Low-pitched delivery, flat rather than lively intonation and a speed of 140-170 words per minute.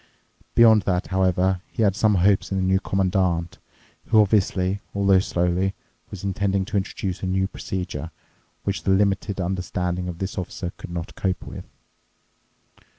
Yes: very low, 95 Hz; narrow, 1.5 semitones; average, 150 wpm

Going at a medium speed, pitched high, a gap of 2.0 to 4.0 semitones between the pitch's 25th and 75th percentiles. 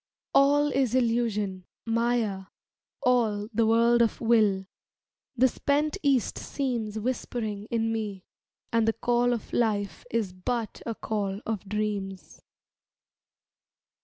No: slow, 115 wpm; high, 225 Hz; average, 2.7 semitones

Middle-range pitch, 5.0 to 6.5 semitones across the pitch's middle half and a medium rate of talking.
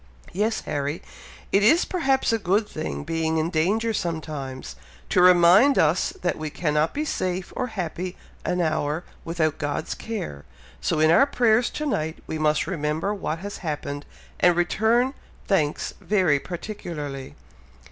Yes: medium, 175 Hz; average, 5.3 semitones; average, 145 wpm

